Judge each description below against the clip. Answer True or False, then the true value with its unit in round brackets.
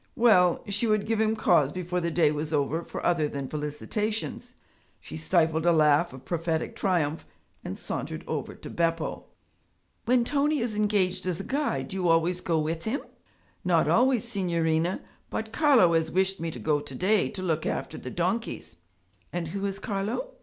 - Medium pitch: True (180 Hz)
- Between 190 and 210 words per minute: False (180 wpm)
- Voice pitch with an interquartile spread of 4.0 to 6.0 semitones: True (4.8 semitones)